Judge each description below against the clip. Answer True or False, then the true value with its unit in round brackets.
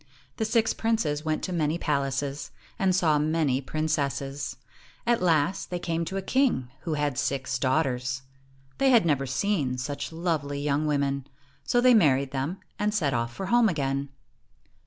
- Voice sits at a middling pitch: True (150 Hz)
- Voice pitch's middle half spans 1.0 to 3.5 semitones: False (4.7 semitones)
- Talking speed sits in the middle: True (160 wpm)